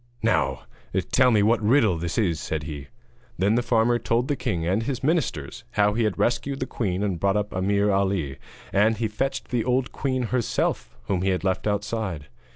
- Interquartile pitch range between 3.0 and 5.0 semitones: Yes, average, 4.3 semitones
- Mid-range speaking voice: No, low, 105 Hz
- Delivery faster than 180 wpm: Yes, average, 195 wpm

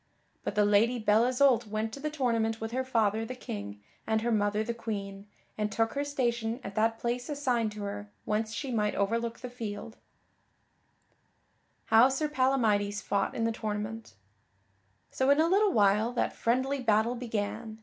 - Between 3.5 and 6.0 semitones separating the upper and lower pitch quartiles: No, average, 3.0 semitones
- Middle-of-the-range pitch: No, high, 225 Hz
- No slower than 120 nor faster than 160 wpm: No, average, 175 wpm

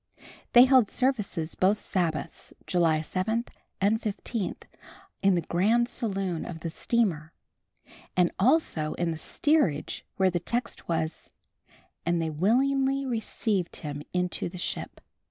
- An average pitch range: No, wide, 5.8 semitones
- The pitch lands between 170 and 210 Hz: Yes, high, 190 Hz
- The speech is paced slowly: Yes, slow, 130 wpm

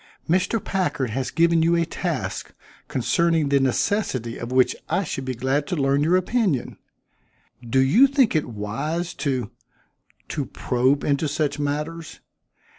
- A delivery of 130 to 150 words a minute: Yes, average, 145 wpm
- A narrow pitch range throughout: No, average, 4.3 semitones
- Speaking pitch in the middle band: Yes, medium, 145 Hz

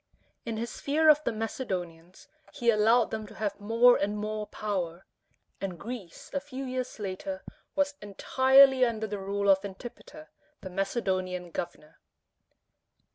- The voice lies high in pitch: Yes, high, 215 Hz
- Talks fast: No, average, 140 wpm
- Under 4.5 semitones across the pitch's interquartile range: No, average, 4.8 semitones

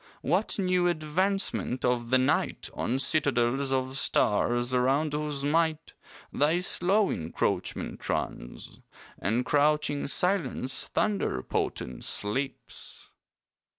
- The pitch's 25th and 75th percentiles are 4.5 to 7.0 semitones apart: Yes, average, 4.8 semitones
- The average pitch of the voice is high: No, medium, 140 Hz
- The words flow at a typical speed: No, slow, 100 wpm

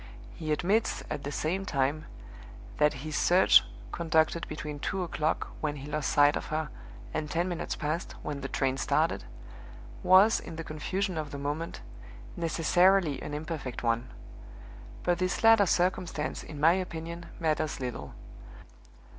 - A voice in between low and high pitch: Yes, medium, 155 Hz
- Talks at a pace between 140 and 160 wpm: Yes, average, 145 wpm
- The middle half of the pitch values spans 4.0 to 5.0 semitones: No, average, 3.0 semitones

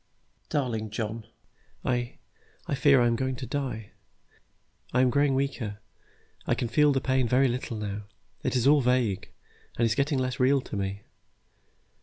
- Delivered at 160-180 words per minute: Yes, average, 170 wpm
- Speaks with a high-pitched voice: No, low, 125 Hz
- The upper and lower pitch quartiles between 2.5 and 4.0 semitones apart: Yes, average, 3.2 semitones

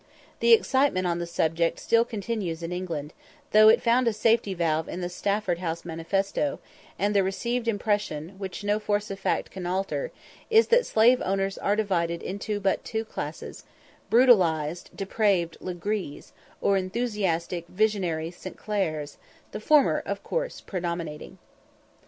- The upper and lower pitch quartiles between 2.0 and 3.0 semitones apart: No, average, 4.1 semitones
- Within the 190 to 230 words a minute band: No, average, 150 wpm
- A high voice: Yes, high, 195 Hz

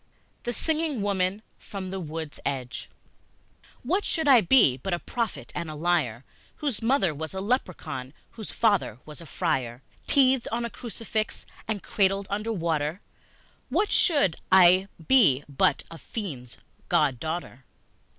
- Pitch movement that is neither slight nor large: No, wide, 7.0 semitones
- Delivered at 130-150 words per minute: Yes, average, 145 wpm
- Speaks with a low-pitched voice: No, high, 190 Hz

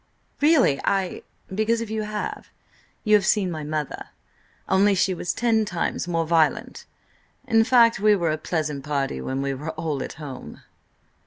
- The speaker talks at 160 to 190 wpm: Yes, average, 165 wpm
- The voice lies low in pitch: No, medium, 175 Hz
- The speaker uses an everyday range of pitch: No, wide, 5.7 semitones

